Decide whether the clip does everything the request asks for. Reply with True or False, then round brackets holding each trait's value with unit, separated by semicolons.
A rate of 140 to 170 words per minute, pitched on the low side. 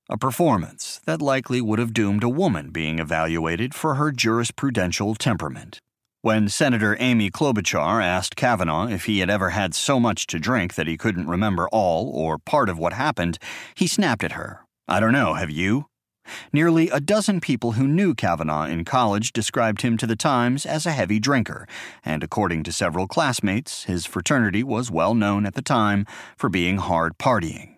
False (180 wpm; 110 Hz)